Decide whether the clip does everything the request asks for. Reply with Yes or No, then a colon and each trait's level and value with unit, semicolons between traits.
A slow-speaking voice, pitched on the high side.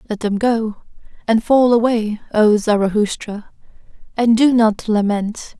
Yes: slow, 130 wpm; high, 220 Hz